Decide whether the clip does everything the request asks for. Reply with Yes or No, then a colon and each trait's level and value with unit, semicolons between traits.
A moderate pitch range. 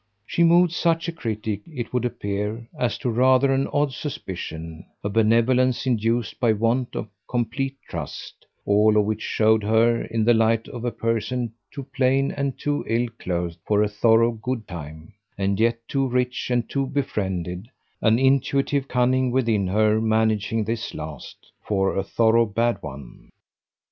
Yes: average, 3.4 semitones